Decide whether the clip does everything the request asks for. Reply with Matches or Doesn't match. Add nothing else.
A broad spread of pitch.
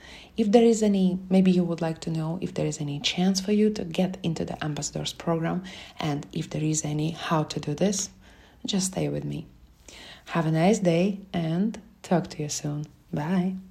Doesn't match